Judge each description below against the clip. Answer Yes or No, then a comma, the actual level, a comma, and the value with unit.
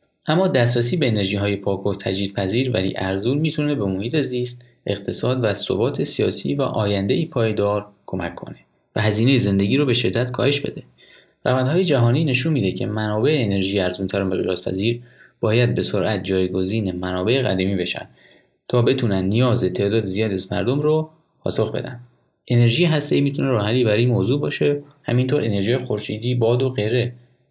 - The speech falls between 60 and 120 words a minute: No, fast, 155 wpm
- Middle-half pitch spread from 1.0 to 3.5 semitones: No, average, 4.3 semitones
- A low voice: Yes, low, 120 Hz